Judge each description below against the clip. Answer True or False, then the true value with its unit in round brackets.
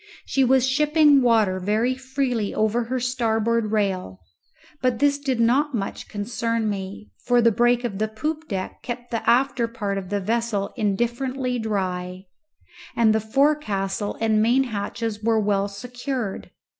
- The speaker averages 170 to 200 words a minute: False (150 wpm)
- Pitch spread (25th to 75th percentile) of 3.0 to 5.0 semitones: True (3.5 semitones)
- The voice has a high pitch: True (230 Hz)